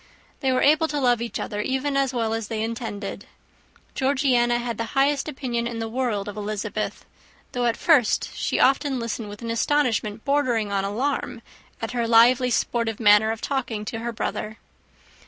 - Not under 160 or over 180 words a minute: Yes, average, 175 wpm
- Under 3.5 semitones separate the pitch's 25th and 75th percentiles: Yes, average, 3.1 semitones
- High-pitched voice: Yes, high, 235 Hz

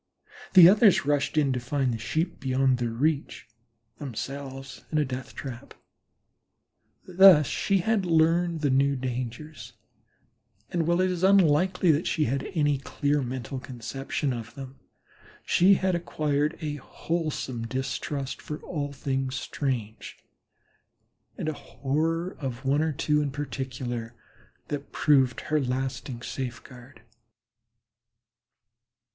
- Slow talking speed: Yes, slow, 125 wpm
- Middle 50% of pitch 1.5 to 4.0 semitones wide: Yes, average, 3.4 semitones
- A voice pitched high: No, medium, 140 Hz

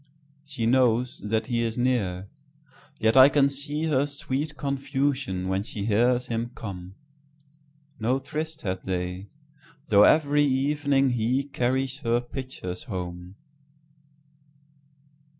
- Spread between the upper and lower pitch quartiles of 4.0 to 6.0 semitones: Yes, average, 4.6 semitones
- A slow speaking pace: Yes, slow, 105 wpm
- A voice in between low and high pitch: No, low, 130 Hz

